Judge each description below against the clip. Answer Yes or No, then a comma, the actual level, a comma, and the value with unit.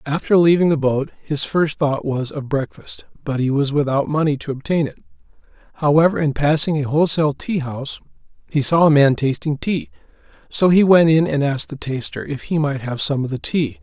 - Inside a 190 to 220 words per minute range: Yes, fast, 205 wpm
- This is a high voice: No, medium, 150 Hz